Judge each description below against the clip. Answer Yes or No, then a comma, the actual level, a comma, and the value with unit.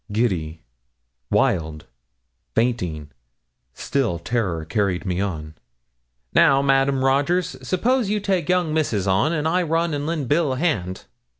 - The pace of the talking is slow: Yes, slow, 130 wpm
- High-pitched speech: No, low, 135 Hz